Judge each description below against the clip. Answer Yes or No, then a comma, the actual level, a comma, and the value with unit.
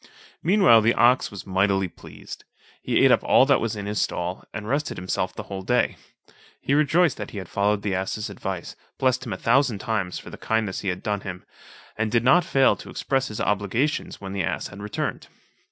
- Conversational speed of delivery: No, fast, 210 wpm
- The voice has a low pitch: Yes, low, 105 Hz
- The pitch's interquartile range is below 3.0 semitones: No, average, 4.5 semitones